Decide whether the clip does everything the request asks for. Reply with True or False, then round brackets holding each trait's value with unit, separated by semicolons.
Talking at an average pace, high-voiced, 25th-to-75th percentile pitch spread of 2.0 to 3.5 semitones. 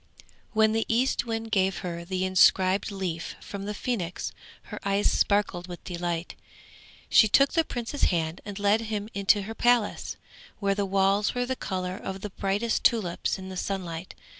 True (165 wpm; 200 Hz; 2.9 semitones)